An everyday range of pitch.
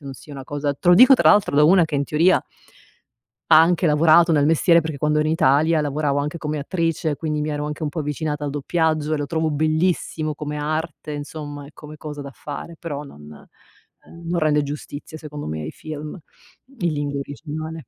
No: narrow, 1.8 semitones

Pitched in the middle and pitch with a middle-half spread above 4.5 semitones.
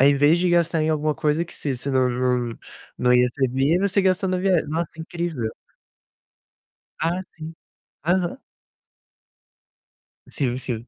Yes: medium, 155 Hz; average, 5.0 semitones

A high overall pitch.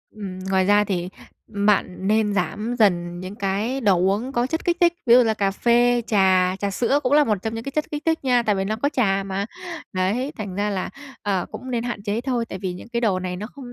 Yes: high, 210 Hz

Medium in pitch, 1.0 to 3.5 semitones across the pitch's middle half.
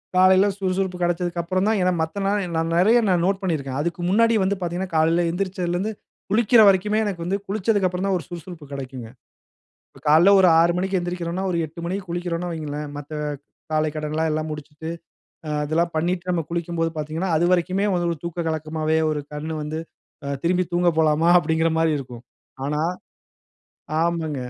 Yes: medium, 170 Hz; average, 2.9 semitones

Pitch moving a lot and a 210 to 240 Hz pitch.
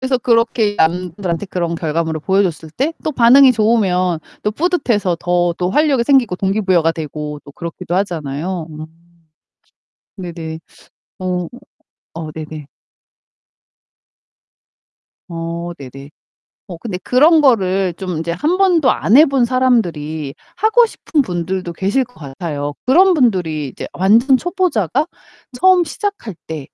No: wide, 7.5 semitones; medium, 185 Hz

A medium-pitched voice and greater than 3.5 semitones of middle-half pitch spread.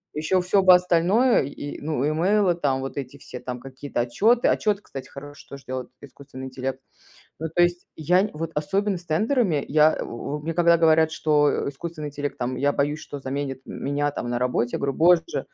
Yes: medium, 150 Hz; average, 4.2 semitones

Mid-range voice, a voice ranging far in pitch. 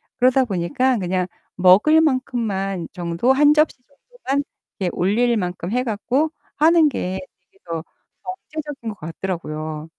No: high, 220 Hz; wide, 7.3 semitones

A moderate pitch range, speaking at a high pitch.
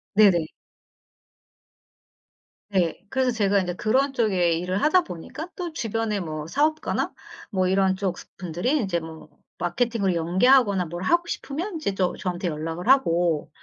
No: wide, 6.3 semitones; high, 195 Hz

